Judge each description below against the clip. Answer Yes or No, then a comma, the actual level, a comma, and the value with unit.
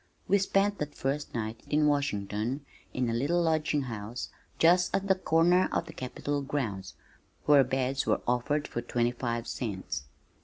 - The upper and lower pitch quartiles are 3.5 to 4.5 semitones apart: No, average, 5.0 semitones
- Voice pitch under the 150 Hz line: Yes, low, 135 Hz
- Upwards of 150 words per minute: Yes, average, 160 wpm